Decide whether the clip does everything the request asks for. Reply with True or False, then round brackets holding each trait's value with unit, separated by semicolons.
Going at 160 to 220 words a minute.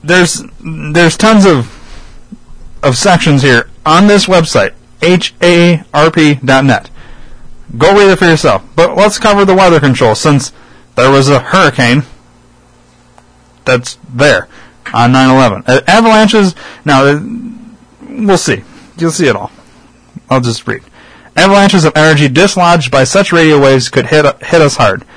False (135 wpm)